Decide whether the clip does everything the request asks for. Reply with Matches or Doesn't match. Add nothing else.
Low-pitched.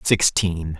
Matches